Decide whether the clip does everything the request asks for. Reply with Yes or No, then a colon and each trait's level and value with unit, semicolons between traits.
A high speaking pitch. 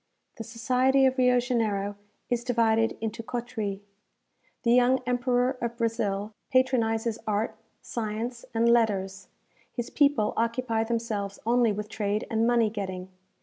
Yes: high, 230 Hz